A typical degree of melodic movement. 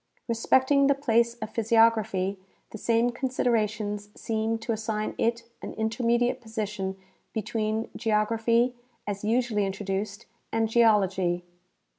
No: narrow, 2.0 semitones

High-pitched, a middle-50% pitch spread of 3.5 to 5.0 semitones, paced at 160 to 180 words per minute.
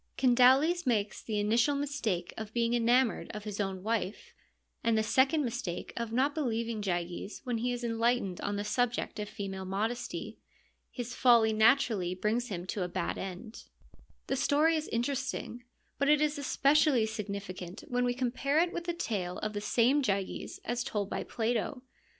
Yes: high, 230 Hz; average, 4.0 semitones; average, 175 wpm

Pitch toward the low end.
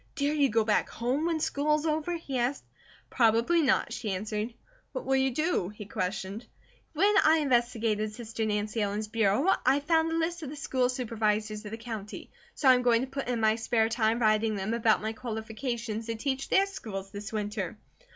No: high, 230 Hz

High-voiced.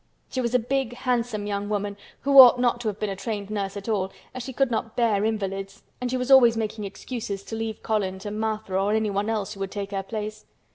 Yes: high, 215 Hz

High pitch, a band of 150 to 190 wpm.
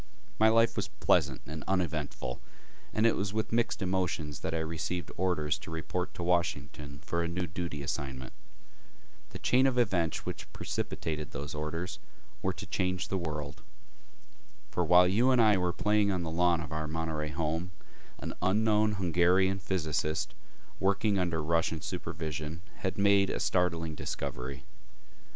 No: very low, 85 Hz; average, 155 wpm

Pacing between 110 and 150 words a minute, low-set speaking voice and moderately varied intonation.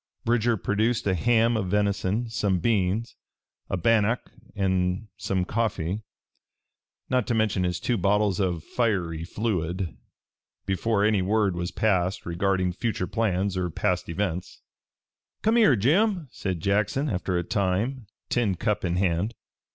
Yes: slow, 135 wpm; low, 100 Hz; average, 3.7 semitones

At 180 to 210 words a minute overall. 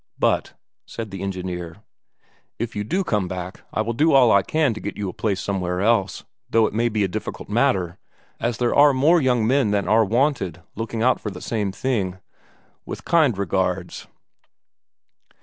Yes: average, 185 wpm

